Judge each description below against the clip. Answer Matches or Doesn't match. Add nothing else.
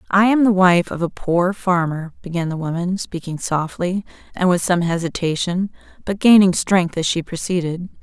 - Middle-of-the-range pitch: Matches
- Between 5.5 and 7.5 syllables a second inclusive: Doesn't match